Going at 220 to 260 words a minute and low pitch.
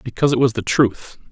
Yes: fast, 230 wpm; low, 120 Hz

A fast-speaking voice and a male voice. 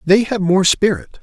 No: average, 195 wpm; male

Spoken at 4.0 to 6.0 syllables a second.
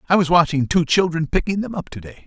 No: 6.2 syllables/s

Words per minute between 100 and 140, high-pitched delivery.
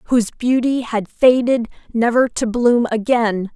Yes: slow, 135 wpm; high, 235 Hz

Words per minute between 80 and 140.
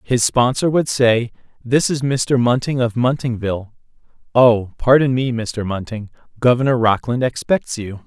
Yes: slow, 135 wpm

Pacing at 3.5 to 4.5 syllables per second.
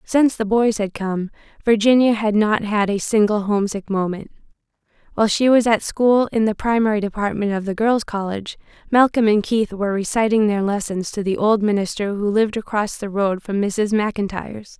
No: 5.4 syllables/s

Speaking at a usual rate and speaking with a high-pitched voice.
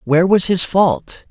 No: average, 185 wpm; medium, 180 Hz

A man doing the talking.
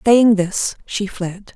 No: female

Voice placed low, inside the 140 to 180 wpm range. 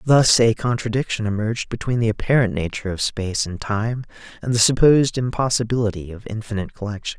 Yes: low, 110 Hz; average, 160 wpm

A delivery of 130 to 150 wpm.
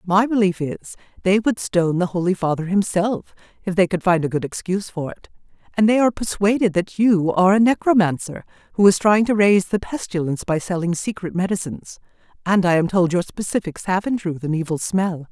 No: average, 195 wpm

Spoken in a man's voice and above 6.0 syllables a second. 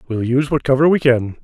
Yes: male; 6.5 syllables/s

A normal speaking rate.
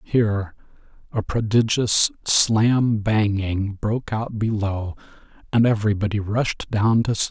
No: slow, 115 wpm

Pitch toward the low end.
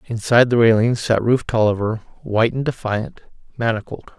Yes: low, 115 Hz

